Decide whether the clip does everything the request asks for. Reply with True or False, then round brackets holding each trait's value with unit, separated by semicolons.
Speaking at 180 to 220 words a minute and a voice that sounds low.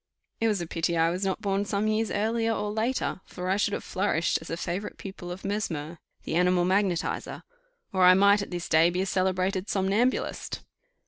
False (200 wpm; 190 Hz)